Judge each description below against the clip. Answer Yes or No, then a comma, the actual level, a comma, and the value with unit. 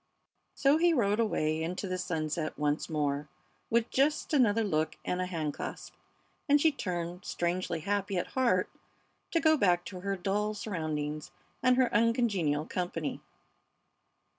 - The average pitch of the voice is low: No, medium, 185 Hz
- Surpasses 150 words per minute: No, average, 145 wpm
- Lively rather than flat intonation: Yes, wide, 6.4 semitones